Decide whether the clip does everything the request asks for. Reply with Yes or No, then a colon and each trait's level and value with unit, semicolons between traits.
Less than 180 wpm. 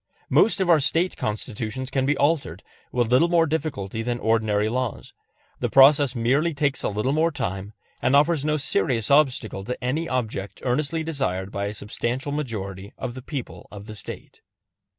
Yes: average, 170 wpm